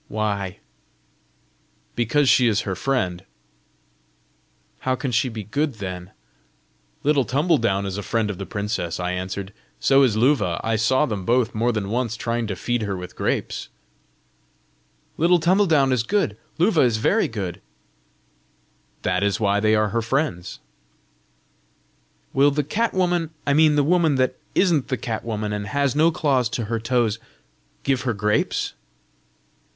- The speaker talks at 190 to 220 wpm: No, average, 155 wpm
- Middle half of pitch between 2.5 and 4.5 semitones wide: No, wide, 5.5 semitones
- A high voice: No, low, 115 Hz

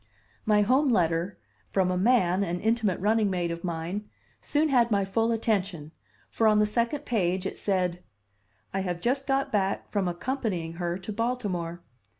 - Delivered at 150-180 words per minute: Yes, average, 165 wpm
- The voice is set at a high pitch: Yes, high, 200 Hz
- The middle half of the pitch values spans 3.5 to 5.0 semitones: Yes, average, 4.3 semitones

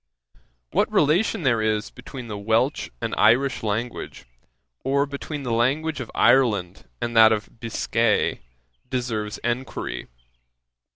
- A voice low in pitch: Yes, low, 120 Hz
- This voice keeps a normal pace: No, slow, 120 wpm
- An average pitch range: Yes, average, 3.6 semitones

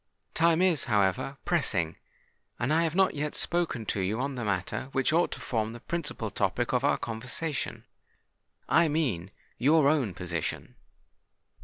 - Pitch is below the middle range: Yes, low, 130 Hz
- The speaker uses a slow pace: No, average, 150 wpm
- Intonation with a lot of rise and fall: Yes, wide, 6.8 semitones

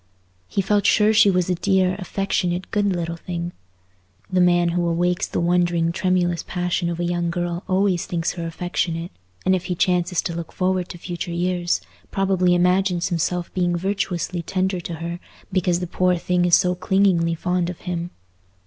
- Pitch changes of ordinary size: No, narrow, 1.2 semitones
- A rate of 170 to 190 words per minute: Yes, average, 175 wpm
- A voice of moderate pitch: Yes, medium, 180 Hz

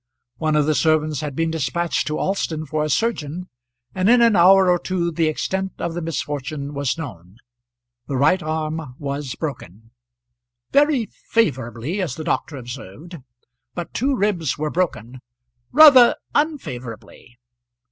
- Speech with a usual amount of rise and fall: Yes, average, 4.9 semitones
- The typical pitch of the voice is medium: Yes, medium, 155 Hz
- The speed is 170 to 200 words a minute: No, average, 145 wpm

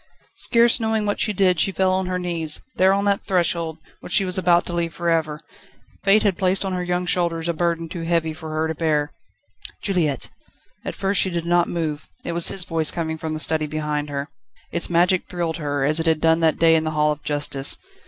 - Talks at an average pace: No, fast, 230 wpm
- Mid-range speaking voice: Yes, medium, 170 Hz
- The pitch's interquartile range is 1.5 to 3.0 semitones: Yes, narrow, 2.5 semitones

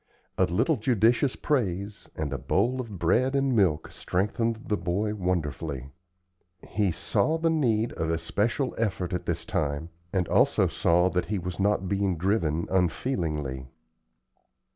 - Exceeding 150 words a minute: No, average, 140 wpm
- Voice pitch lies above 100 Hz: No, very low, 95 Hz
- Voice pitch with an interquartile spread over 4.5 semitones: Yes, average, 5.2 semitones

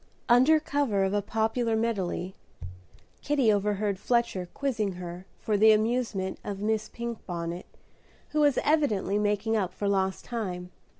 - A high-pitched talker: Yes, high, 210 Hz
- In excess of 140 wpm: No, slow, 135 wpm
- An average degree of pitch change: Yes, average, 3.6 semitones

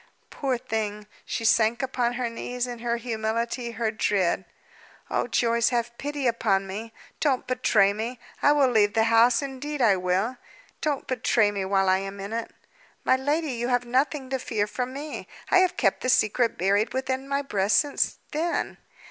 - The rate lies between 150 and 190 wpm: Yes, average, 180 wpm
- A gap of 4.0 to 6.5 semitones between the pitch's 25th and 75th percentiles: No, average, 3.4 semitones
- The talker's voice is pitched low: No, high, 235 Hz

